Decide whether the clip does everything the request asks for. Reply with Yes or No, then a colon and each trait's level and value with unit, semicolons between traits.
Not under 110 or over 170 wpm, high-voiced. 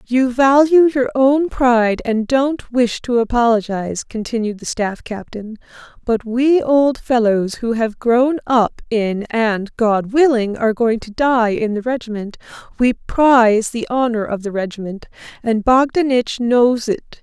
Yes: average, 155 wpm; high, 235 Hz